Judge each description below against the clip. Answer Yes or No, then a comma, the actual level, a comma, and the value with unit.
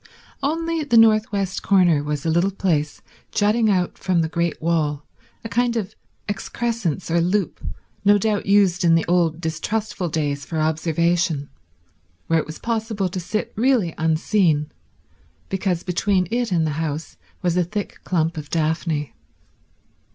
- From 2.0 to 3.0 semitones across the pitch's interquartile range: No, average, 4.3 semitones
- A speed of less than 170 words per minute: Yes, average, 150 wpm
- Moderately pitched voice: Yes, medium, 175 Hz